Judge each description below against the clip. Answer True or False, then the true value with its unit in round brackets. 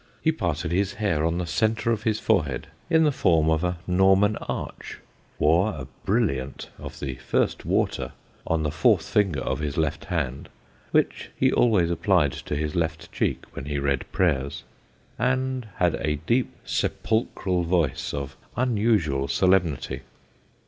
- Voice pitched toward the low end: True (85 Hz)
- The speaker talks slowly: False (155 wpm)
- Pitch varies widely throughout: True (6.0 semitones)